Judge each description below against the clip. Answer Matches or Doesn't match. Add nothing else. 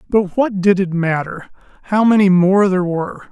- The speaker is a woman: Doesn't match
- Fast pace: Doesn't match